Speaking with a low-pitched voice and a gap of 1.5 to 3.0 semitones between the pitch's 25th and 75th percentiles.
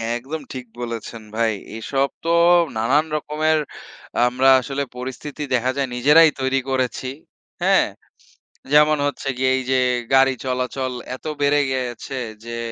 Yes: low, 130 Hz; narrow, 2.4 semitones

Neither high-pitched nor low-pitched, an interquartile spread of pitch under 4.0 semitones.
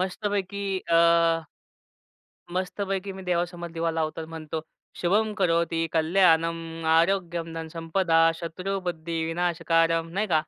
Yes: medium, 170 Hz; narrow, 2.4 semitones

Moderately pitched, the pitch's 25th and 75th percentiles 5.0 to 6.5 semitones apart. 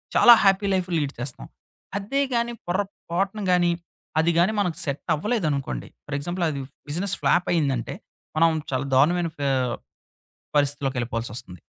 Yes: medium, 165 Hz; wide, 5.5 semitones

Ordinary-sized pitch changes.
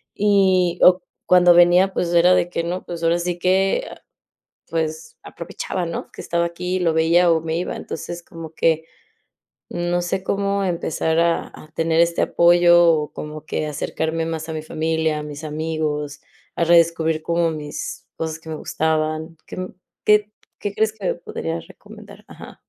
No: narrow, 1.9 semitones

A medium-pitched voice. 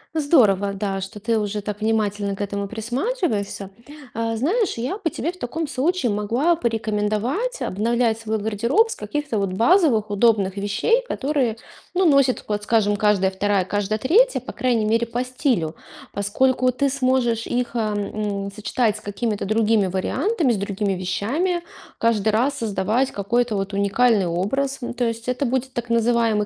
No: high, 225 Hz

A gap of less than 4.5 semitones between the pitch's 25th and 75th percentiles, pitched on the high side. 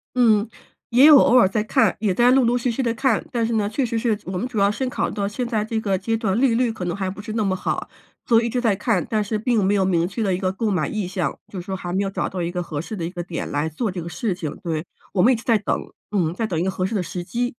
Yes: average, 3.9 semitones; high, 210 Hz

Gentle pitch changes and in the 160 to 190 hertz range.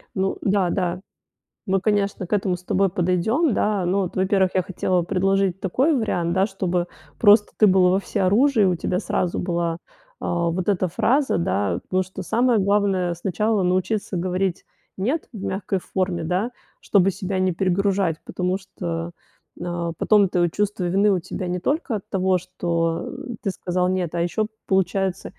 Yes: narrow, 2.1 semitones; medium, 185 Hz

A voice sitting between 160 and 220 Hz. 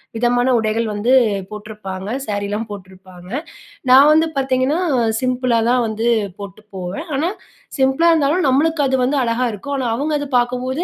No: high, 245 Hz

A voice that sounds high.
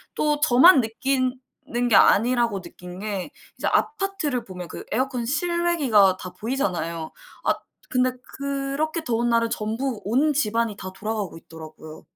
Yes: high, 235 Hz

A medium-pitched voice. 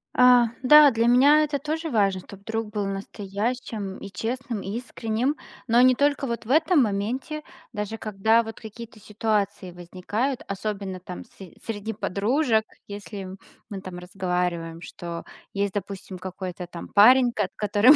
No: high, 215 Hz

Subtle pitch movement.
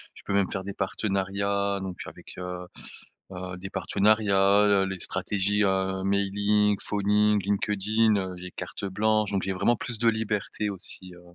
Yes: narrow, 1.5 semitones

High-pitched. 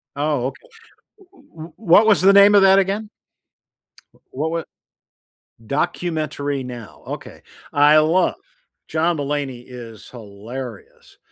No: medium, 155 Hz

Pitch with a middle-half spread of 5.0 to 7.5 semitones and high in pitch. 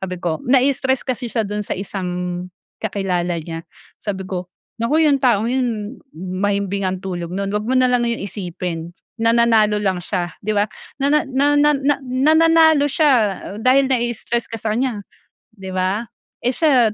Yes: wide, 5.5 semitones; high, 220 Hz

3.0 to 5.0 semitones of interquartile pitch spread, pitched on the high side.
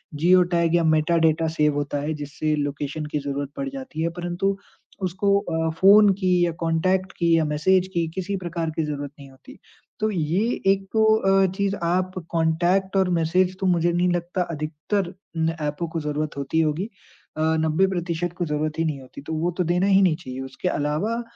No: average, 3.5 semitones; medium, 170 Hz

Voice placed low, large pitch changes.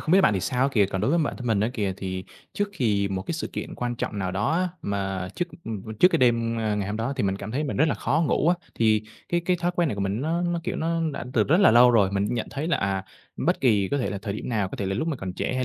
Yes: low, 115 Hz; wide, 7.3 semitones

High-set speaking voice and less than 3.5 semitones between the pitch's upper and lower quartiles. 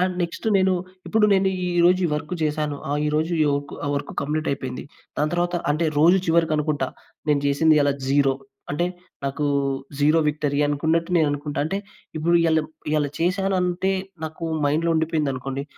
No: medium, 155 Hz; average, 2.9 semitones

